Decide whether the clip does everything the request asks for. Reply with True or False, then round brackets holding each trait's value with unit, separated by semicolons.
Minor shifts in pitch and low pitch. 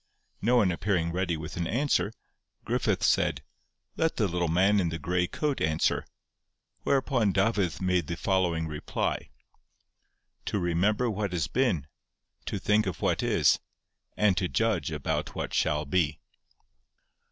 False (4.2 semitones; 90 Hz)